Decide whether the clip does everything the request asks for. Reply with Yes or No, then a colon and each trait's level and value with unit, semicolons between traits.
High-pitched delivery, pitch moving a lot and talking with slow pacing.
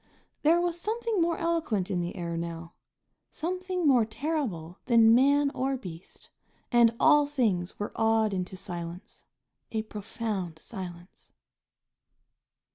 Yes: high, 225 Hz; wide, 8.6 semitones; slow, 120 wpm